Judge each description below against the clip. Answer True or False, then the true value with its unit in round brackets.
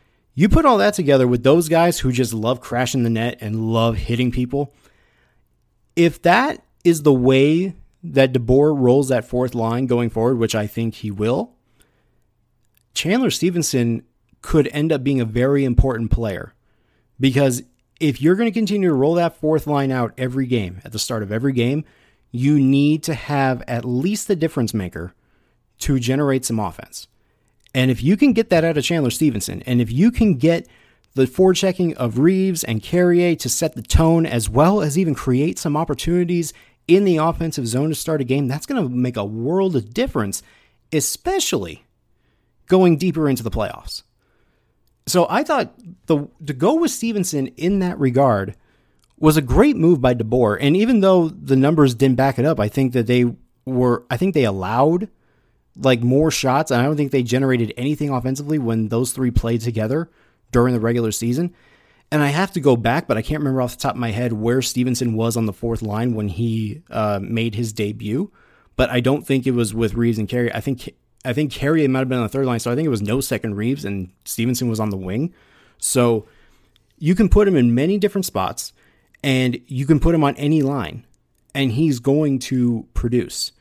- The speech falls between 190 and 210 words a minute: True (200 wpm)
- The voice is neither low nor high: False (130 Hz)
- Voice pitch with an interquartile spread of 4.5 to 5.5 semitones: True (4.9 semitones)